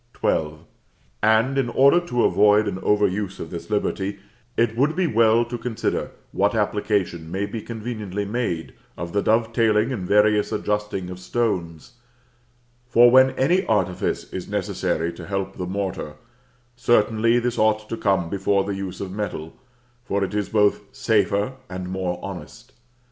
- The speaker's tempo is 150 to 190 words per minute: Yes, average, 155 wpm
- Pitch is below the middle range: Yes, low, 105 Hz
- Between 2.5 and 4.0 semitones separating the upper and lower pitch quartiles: Yes, average, 3.3 semitones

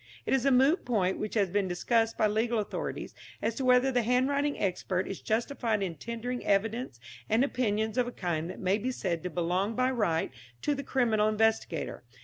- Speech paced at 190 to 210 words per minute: Yes, average, 195 wpm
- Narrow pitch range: No, average, 4.2 semitones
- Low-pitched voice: No, high, 225 Hz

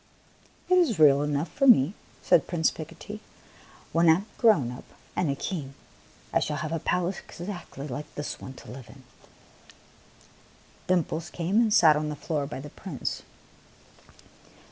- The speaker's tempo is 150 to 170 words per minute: Yes, average, 165 wpm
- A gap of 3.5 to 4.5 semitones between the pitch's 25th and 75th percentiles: Yes, average, 4.0 semitones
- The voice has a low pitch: No, medium, 160 Hz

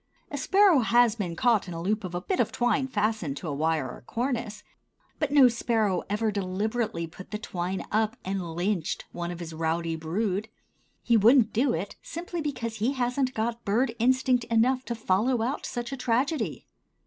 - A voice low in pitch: No, high, 220 Hz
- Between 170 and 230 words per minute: Yes, average, 190 wpm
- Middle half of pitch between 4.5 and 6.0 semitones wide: Yes, average, 5.1 semitones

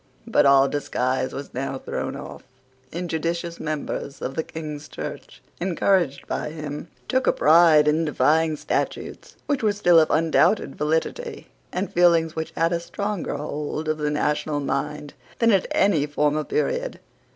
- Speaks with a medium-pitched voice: Yes, medium, 155 Hz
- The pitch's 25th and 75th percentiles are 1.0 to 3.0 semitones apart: Yes, average, 2.7 semitones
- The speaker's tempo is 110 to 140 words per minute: No, average, 150 wpm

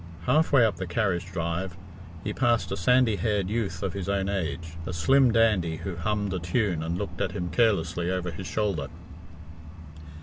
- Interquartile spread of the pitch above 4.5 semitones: No, average, 4.0 semitones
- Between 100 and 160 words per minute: No, average, 180 wpm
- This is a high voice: No, very low, 95 Hz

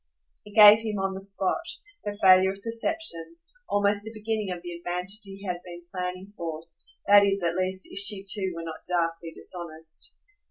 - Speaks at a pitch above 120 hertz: Yes, high, 190 Hz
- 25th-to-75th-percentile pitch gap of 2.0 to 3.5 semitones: Yes, average, 2.7 semitones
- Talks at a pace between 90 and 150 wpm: No, average, 185 wpm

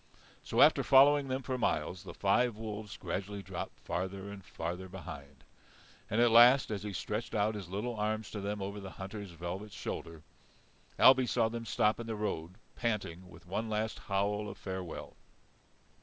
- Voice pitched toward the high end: No, low, 105 Hz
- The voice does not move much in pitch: No, average, 3.1 semitones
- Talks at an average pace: Yes, average, 170 wpm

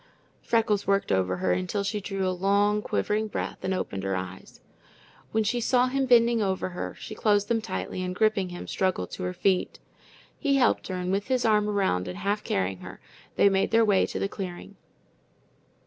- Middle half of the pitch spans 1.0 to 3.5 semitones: Yes, average, 3.1 semitones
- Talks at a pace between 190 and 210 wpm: Yes, average, 195 wpm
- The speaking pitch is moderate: No, high, 195 Hz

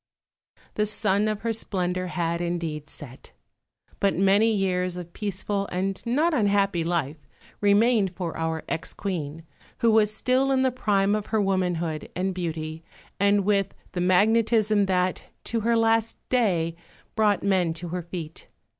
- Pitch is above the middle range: Yes, high, 195 Hz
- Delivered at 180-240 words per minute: No, average, 150 wpm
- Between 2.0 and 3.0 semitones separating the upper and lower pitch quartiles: No, average, 3.6 semitones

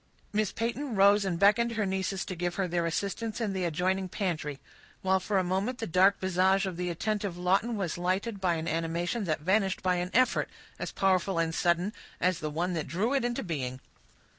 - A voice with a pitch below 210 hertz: Yes, medium, 185 Hz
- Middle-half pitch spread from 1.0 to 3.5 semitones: Yes, average, 2.8 semitones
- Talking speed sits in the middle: No, fast, 210 wpm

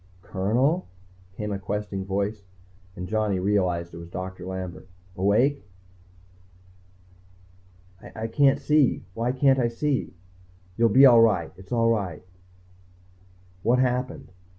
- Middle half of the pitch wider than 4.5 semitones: Yes, average, 4.9 semitones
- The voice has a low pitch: Yes, low, 105 Hz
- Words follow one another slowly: Yes, slow, 120 wpm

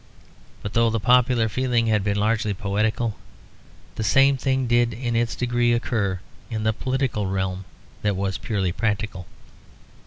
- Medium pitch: No, low, 110 Hz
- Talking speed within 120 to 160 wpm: Yes, average, 150 wpm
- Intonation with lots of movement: No, average, 2.9 semitones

